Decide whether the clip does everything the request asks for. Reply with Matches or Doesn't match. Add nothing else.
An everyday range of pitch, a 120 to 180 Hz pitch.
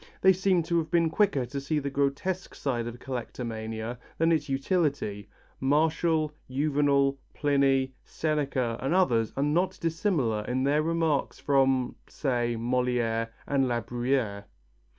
Matches